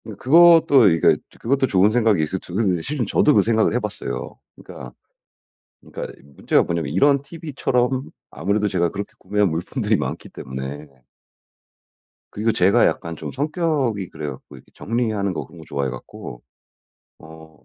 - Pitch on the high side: No, low, 105 Hz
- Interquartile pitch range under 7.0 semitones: No, wide, 7.3 semitones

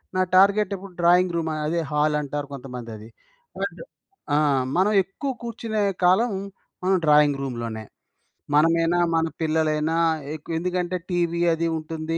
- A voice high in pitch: No, medium, 165 Hz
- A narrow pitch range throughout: No, average, 3.5 semitones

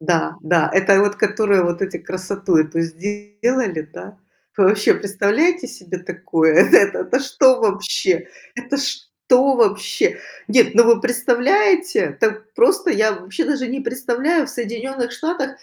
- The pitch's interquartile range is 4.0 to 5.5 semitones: Yes, average, 5.2 semitones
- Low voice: No, high, 215 Hz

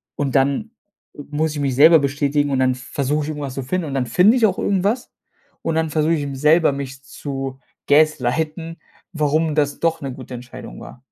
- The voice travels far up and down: No, average, 2.9 semitones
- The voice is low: No, medium, 145 Hz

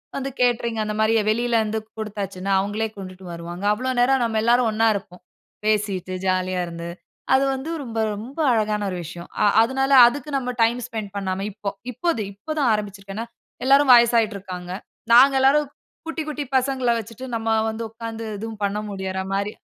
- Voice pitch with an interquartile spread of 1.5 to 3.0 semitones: No, average, 3.7 semitones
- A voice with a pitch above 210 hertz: Yes, high, 220 Hz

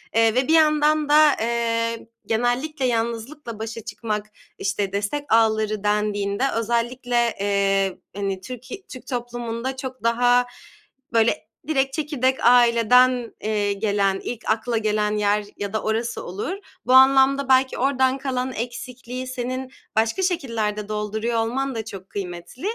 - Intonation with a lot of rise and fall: No, average, 3.3 semitones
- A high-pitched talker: Yes, high, 235 Hz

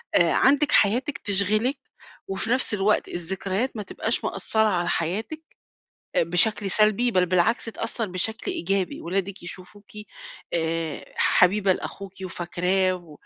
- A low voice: No, high, 195 Hz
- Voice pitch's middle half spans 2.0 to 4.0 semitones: Yes, average, 3.4 semitones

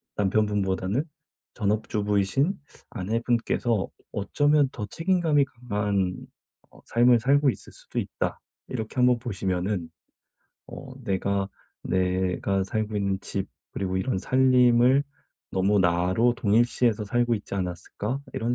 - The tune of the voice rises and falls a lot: No, average, 4.2 semitones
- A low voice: Yes, low, 105 Hz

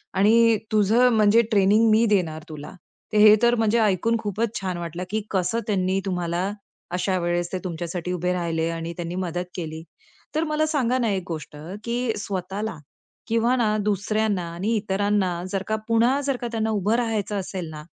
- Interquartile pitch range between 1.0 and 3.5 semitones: No, average, 4.1 semitones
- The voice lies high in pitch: Yes, high, 200 Hz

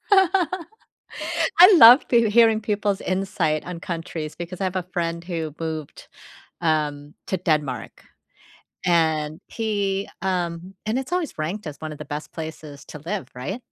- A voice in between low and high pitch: Yes, medium, 175 Hz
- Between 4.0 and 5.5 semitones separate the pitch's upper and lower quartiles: Yes, average, 5.1 semitones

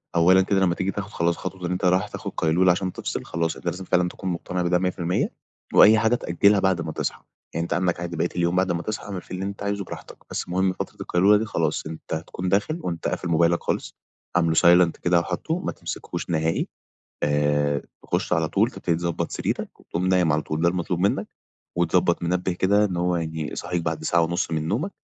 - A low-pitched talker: Yes, very low, 90 Hz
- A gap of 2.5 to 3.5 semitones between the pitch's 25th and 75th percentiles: No, narrow, 2.0 semitones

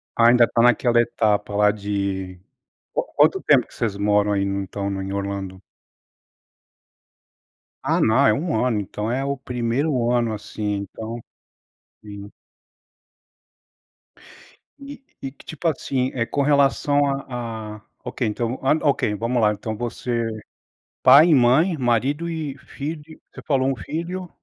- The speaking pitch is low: Yes, low, 120 Hz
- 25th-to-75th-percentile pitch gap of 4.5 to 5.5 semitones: Yes, average, 4.8 semitones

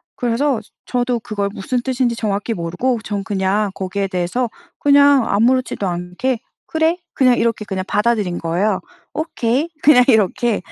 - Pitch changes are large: No, average, 4.3 semitones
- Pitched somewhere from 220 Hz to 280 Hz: Yes, high, 230 Hz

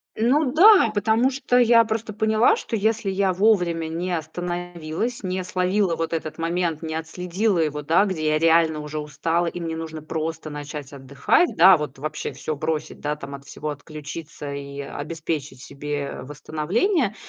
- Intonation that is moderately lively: Yes, average, 4.6 semitones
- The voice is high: No, medium, 165 Hz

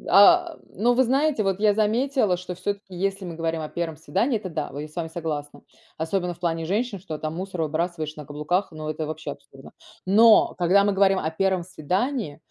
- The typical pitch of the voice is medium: Yes, medium, 180 Hz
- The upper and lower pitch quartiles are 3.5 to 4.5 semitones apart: Yes, average, 4.0 semitones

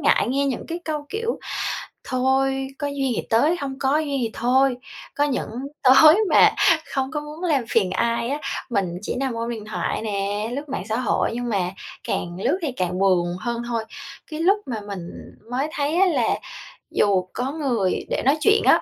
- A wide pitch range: No, average, 4.8 semitones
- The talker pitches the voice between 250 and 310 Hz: Yes, very high, 260 Hz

